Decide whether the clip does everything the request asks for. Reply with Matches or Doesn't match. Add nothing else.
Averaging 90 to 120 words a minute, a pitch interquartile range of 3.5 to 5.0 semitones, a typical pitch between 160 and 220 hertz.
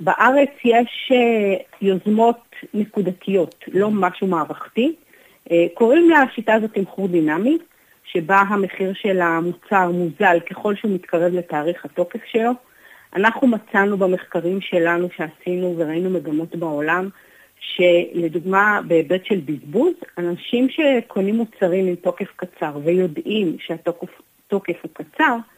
Matches